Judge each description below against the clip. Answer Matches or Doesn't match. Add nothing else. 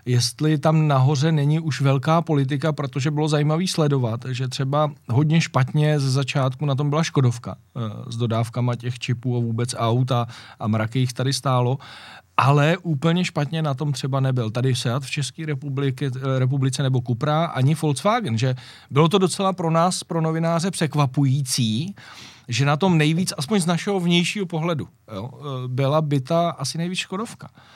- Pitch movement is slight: Doesn't match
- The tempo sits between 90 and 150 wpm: Doesn't match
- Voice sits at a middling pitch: Matches